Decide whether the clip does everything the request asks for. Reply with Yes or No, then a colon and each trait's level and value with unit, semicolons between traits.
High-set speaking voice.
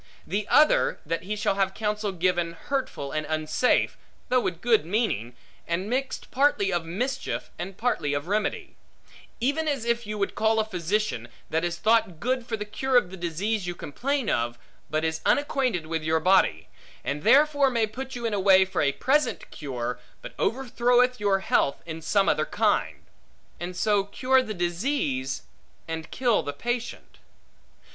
Yes: high, 200 Hz